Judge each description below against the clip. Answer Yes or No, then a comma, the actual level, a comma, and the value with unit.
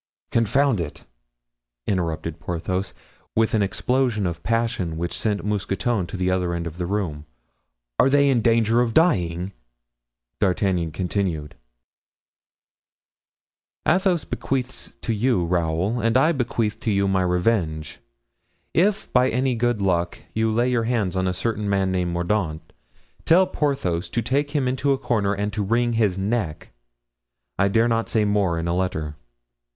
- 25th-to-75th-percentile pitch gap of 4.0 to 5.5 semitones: Yes, average, 5.1 semitones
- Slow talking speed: No, average, 150 wpm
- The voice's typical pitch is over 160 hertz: No, low, 100 Hz